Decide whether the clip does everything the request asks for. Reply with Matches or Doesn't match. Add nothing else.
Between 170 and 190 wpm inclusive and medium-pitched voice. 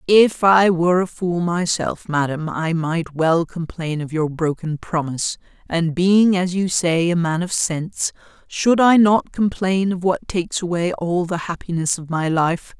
Matches